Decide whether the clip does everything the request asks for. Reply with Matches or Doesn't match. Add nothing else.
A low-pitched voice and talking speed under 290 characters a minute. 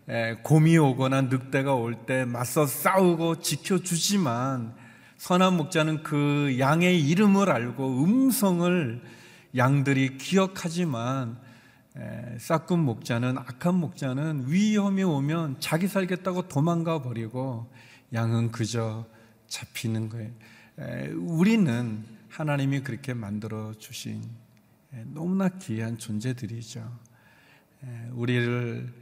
Matches